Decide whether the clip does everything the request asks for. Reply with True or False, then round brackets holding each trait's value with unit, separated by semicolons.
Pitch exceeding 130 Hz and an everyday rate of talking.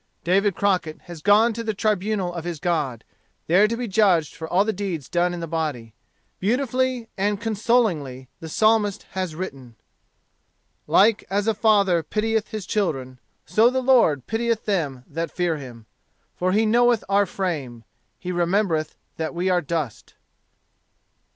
True (185 Hz; 155 wpm)